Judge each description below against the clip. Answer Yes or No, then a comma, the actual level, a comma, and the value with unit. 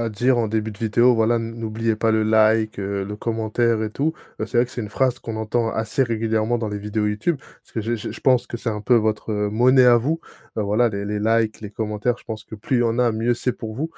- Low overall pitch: Yes, low, 110 Hz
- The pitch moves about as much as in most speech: No, narrow, 1.9 semitones